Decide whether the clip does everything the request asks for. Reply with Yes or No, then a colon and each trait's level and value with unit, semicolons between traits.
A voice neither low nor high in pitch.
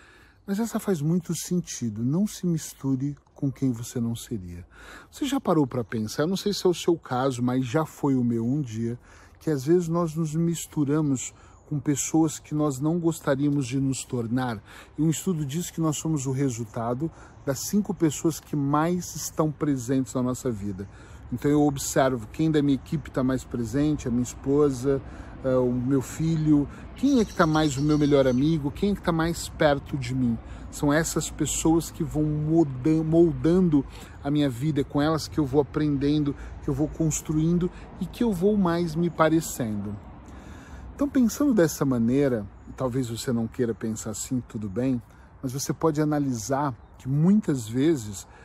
Yes: medium, 145 Hz